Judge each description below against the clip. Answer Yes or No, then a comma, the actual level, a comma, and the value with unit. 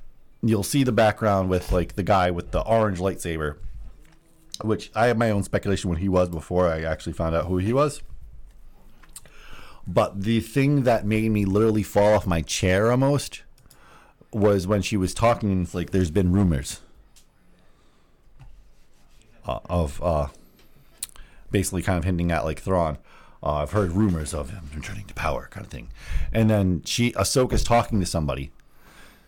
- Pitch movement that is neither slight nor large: Yes, average, 4.3 semitones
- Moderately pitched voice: No, very low, 95 Hz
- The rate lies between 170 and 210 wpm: No, average, 160 wpm